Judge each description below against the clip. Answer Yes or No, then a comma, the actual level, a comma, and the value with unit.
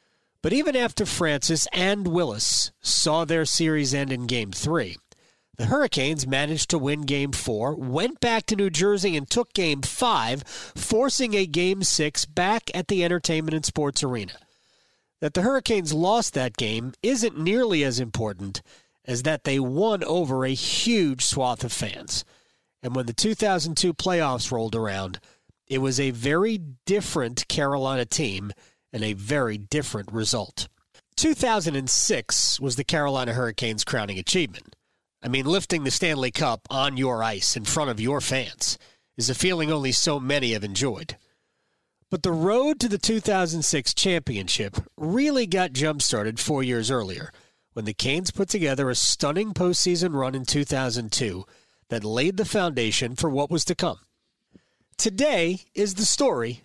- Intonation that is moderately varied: No, wide, 6.4 semitones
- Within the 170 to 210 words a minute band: No, average, 155 wpm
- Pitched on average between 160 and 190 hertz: No, medium, 145 Hz